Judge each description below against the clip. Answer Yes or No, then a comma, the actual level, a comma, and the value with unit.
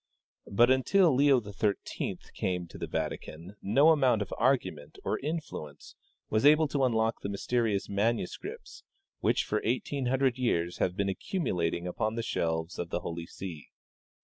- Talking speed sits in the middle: Yes, average, 150 wpm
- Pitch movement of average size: No, wide, 6.8 semitones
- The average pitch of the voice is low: Yes, low, 110 Hz